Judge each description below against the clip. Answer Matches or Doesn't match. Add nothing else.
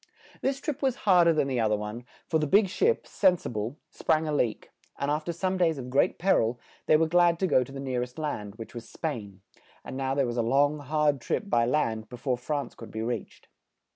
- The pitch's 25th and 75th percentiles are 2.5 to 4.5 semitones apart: Doesn't match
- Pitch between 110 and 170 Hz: Matches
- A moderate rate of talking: Doesn't match